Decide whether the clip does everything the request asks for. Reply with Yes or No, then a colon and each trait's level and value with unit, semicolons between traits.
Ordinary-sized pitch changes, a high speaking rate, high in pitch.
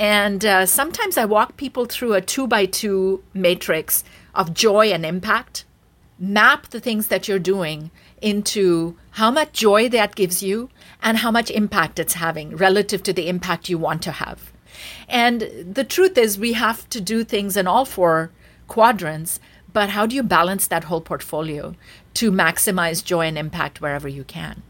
No: average, 4.4 semitones; average, 175 wpm; high, 195 Hz